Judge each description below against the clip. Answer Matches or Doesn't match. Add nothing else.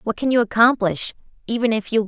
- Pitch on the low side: Doesn't match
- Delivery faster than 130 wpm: Matches